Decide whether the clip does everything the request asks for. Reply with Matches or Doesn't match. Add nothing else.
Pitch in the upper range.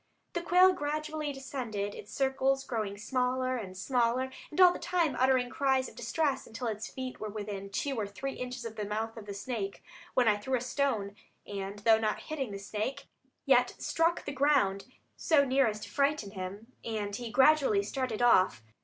Matches